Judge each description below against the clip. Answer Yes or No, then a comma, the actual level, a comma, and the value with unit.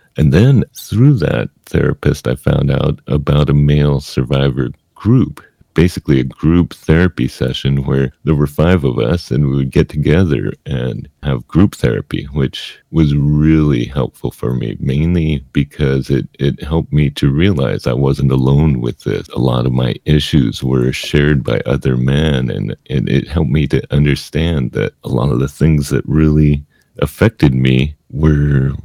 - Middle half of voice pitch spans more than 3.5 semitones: No, narrow, 2.4 semitones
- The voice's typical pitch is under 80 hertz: Yes, very low, 70 Hz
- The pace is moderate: Yes, average, 165 wpm